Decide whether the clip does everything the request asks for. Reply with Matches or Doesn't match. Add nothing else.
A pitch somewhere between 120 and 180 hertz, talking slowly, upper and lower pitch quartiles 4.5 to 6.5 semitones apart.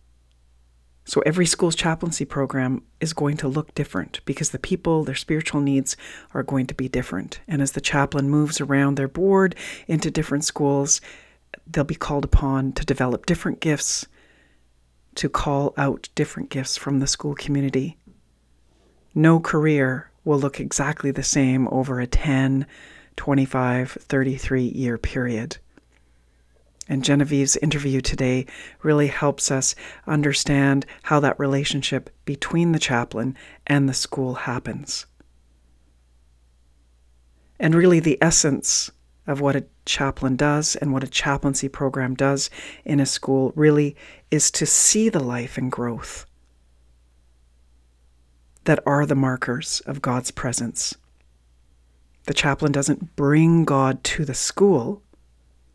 Matches